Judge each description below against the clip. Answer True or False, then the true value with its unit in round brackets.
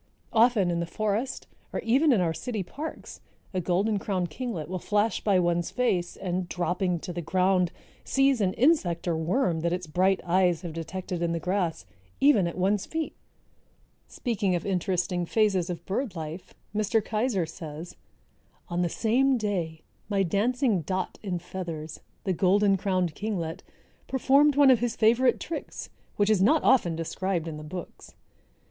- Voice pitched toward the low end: False (185 Hz)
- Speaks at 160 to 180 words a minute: True (165 wpm)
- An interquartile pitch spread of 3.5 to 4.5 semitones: True (4.1 semitones)